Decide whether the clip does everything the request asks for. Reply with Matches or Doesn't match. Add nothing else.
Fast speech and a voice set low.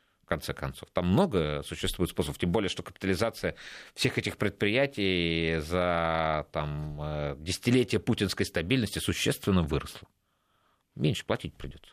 Doesn't match